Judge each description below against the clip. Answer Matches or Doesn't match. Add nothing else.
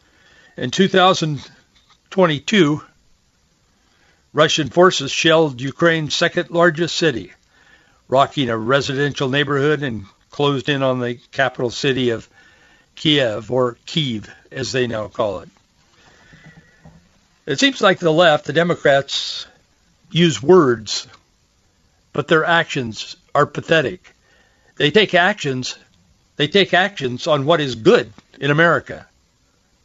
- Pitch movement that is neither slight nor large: Matches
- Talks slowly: Matches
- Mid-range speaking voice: Matches